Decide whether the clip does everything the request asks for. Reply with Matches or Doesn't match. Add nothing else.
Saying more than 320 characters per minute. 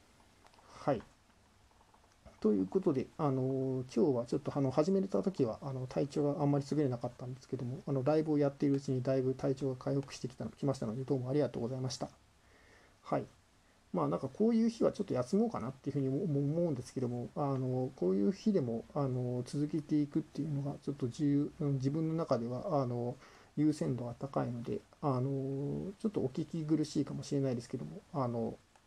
Matches